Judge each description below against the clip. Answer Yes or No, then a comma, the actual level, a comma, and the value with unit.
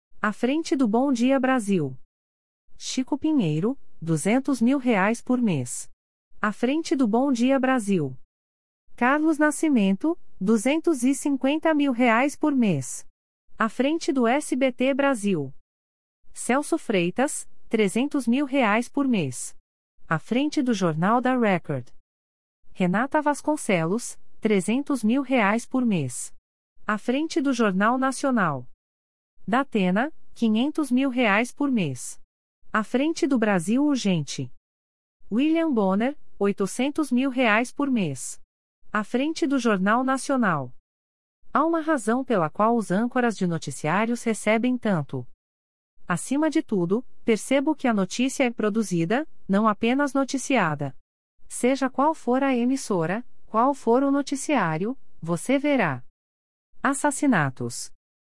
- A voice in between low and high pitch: No, high, 230 Hz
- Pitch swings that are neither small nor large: No, wide, 9.0 semitones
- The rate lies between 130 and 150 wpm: No, slow, 120 wpm